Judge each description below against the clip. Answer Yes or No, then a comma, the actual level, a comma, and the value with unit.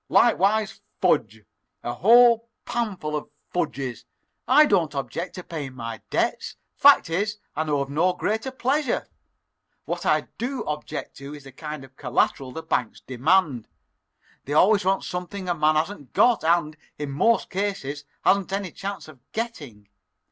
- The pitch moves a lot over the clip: Yes, wide, 6.3 semitones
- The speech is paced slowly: No, average, 155 wpm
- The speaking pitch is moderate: Yes, medium, 165 Hz